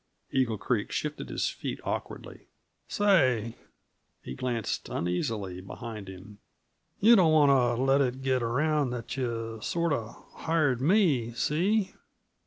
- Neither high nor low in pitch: No, low, 125 Hz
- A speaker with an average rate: No, slow, 130 wpm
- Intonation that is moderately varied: Yes, average, 5.0 semitones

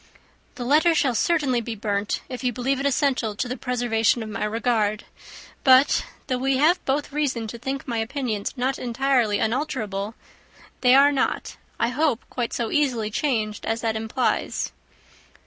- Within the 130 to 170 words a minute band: Yes, average, 165 wpm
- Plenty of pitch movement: No, average, 3.5 semitones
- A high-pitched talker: Yes, very high, 250 Hz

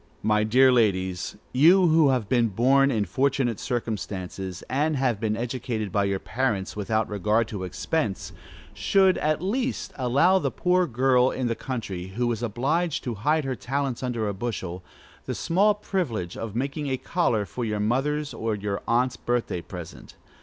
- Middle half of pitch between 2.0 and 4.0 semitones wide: No, average, 4.7 semitones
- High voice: No, low, 120 Hz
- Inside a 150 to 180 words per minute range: Yes, average, 165 wpm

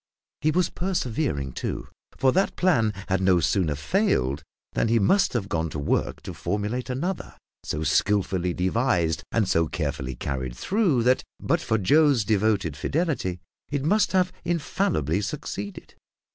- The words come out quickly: No, average, 145 wpm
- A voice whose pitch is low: Yes, low, 105 Hz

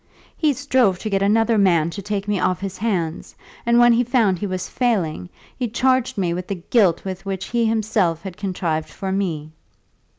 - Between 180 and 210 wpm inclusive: Yes, average, 195 wpm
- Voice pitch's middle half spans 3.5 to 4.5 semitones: Yes, average, 4.1 semitones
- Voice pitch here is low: No, high, 195 Hz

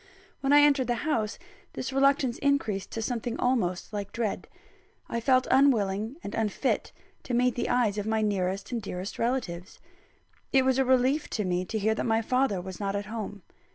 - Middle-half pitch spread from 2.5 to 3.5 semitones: No, average, 4.3 semitones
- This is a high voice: Yes, high, 225 Hz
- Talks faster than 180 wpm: Yes, average, 190 wpm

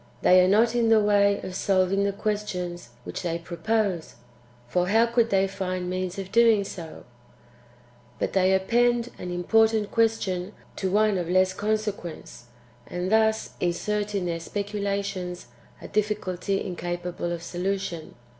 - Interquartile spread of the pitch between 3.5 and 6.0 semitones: No, average, 2.9 semitones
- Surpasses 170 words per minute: No, average, 145 wpm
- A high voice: Yes, high, 195 Hz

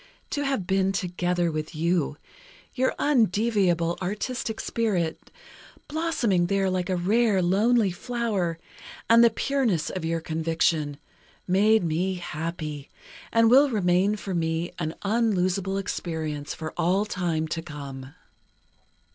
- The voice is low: No, medium, 185 Hz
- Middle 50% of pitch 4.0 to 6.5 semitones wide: Yes, average, 4.7 semitones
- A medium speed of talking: No, slow, 120 wpm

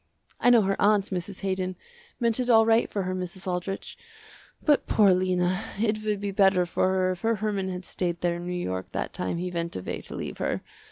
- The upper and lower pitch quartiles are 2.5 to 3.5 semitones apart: Yes, average, 2.8 semitones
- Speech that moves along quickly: Yes, fast, 220 wpm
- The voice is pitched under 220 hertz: Yes, high, 190 Hz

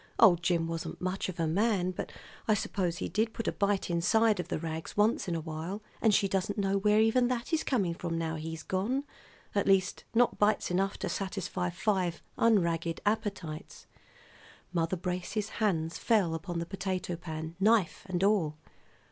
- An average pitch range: Yes, average, 3.8 semitones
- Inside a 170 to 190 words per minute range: Yes, average, 180 wpm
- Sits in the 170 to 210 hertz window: Yes, medium, 185 Hz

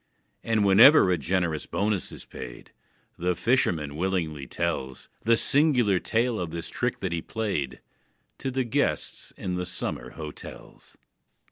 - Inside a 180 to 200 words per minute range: No, average, 140 wpm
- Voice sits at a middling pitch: No, very low, 95 Hz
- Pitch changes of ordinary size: No, wide, 6.0 semitones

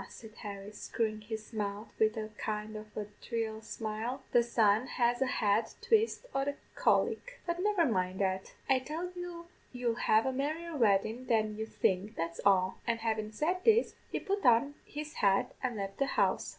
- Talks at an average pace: Yes, average, 185 wpm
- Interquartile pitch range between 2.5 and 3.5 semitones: No, average, 4.7 semitones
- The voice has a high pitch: Yes, high, 225 Hz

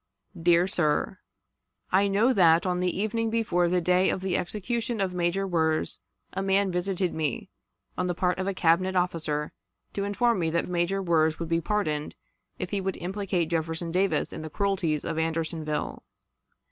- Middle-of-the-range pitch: Yes, medium, 180 Hz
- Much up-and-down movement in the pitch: No, average, 2.9 semitones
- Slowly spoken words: No, average, 170 wpm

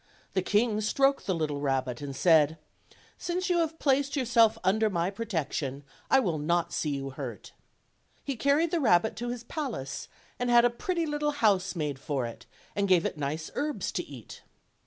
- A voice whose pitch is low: No, high, 205 Hz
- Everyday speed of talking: Yes, average, 185 wpm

